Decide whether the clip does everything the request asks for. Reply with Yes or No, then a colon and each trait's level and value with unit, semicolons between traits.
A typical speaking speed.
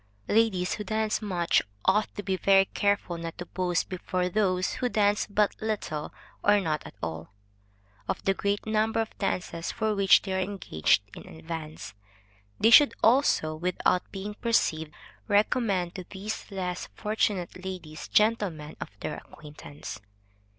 Yes: average, 150 wpm